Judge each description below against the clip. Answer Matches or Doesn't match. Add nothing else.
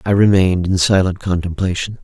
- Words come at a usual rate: Matches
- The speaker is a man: Matches